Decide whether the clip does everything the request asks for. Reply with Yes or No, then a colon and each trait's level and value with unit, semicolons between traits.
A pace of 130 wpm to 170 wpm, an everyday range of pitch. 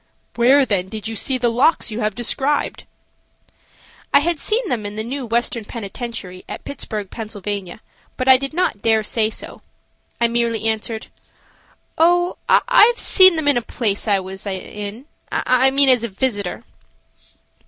Yes: average, 160 wpm; average, 4.3 semitones